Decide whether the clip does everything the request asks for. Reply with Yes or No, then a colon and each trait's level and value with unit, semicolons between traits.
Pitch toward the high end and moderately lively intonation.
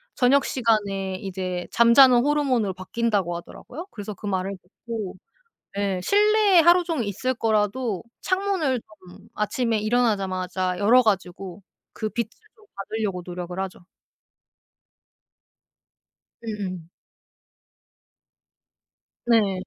Yes: high, 210 Hz; average, 4.7 semitones